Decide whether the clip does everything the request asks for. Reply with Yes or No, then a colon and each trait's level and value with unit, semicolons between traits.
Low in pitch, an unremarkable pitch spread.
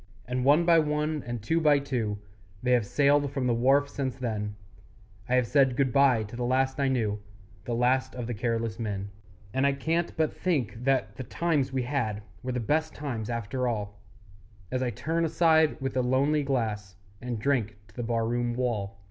Yes: low, 125 Hz; average, 3.6 semitones